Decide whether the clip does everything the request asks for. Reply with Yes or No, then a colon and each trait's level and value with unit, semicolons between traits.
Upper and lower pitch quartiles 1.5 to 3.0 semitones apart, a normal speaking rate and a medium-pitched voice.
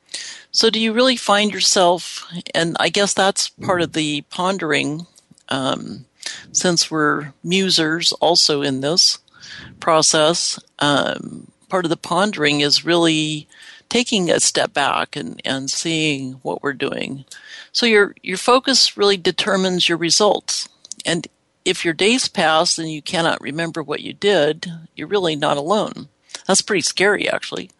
No: average, 4.5 semitones; average, 145 wpm; medium, 170 Hz